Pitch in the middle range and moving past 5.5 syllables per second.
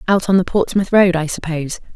Yes: medium, 180 Hz; 6.0 syllables/s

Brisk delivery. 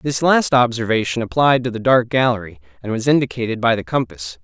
No: average, 190 wpm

